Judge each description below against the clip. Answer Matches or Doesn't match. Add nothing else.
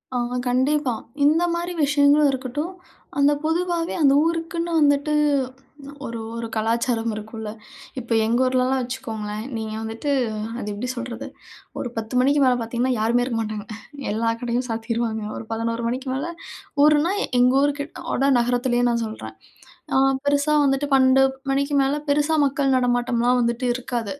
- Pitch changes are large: Doesn't match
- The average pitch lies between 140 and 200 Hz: Doesn't match